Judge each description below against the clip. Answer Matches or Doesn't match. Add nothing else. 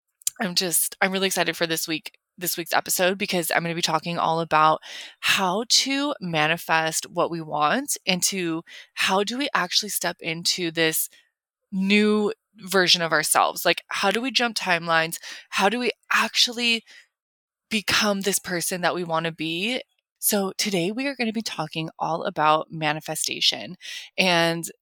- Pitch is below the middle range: Doesn't match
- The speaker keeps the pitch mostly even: Doesn't match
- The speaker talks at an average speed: Matches